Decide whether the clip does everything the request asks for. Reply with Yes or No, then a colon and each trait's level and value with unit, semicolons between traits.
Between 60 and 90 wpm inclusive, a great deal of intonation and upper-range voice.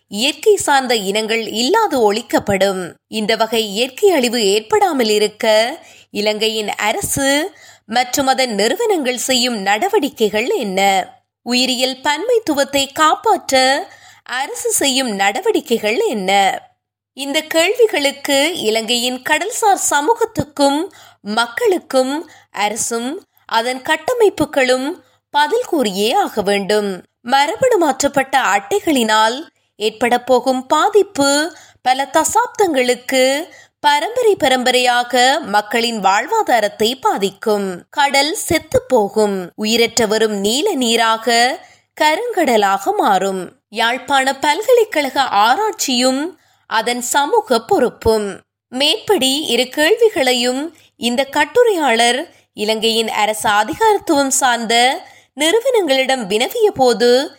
Yes: average, 80 wpm; wide, 6.9 semitones; very high, 265 Hz